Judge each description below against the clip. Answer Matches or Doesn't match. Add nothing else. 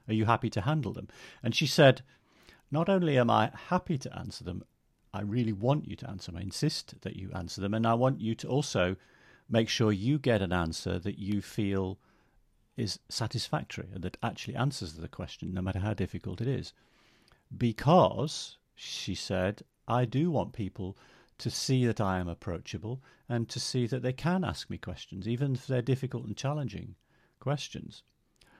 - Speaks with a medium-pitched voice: Doesn't match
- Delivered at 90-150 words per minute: Doesn't match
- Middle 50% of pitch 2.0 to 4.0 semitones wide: Doesn't match